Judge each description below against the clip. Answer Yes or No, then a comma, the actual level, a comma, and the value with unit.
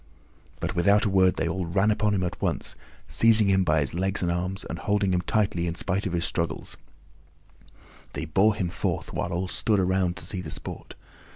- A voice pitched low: Yes, very low, 95 Hz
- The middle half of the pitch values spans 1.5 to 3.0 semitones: Yes, narrow, 2.5 semitones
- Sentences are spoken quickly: Yes, fast, 210 wpm